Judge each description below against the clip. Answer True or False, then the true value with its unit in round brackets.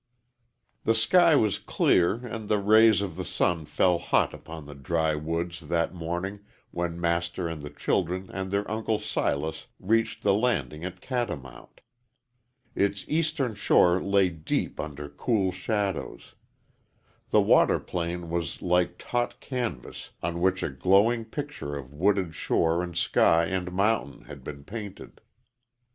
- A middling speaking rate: True (145 wpm)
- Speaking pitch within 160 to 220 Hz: False (90 Hz)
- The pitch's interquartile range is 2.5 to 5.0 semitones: True (4.1 semitones)